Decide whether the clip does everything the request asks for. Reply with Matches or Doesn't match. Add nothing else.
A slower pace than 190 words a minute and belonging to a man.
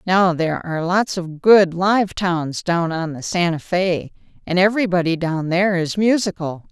Doesn't match